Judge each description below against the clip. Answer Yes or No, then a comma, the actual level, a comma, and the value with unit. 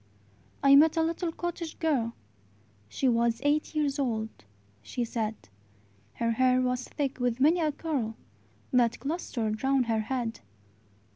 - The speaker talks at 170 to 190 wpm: No, average, 140 wpm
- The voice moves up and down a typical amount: Yes, average, 4.5 semitones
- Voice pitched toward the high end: Yes, very high, 255 Hz